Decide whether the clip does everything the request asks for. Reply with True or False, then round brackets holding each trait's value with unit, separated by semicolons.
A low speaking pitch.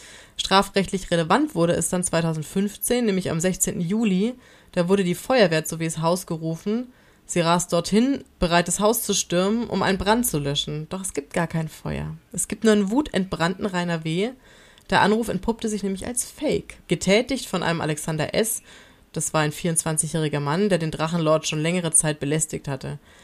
False (175 Hz)